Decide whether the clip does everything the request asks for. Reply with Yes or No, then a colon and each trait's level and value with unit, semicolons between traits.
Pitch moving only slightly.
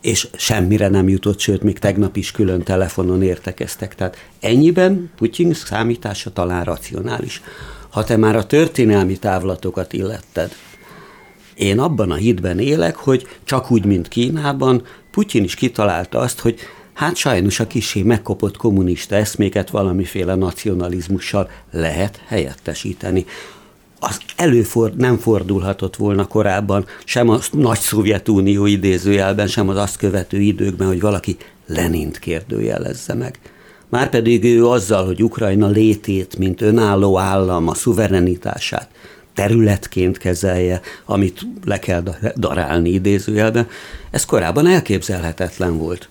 No: average, 3.4 semitones